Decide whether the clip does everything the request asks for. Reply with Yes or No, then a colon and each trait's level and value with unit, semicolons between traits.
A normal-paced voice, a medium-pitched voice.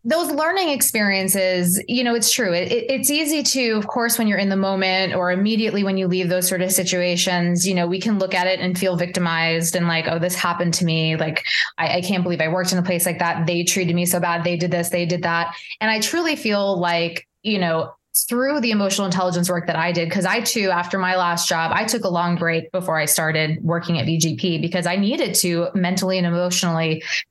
No: fast, 235 wpm; medium, 180 Hz